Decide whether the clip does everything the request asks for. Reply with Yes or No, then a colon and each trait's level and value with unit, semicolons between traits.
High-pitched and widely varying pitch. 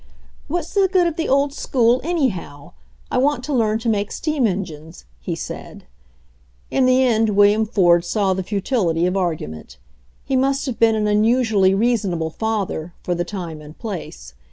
Yes: high, 210 Hz; wide, 6.5 semitones